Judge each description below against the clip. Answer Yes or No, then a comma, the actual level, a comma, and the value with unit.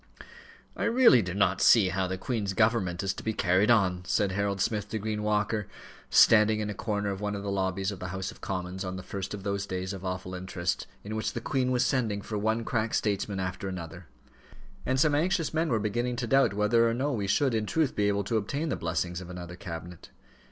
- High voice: No, low, 100 Hz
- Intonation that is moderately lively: Yes, average, 3.4 semitones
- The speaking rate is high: Yes, fast, 230 wpm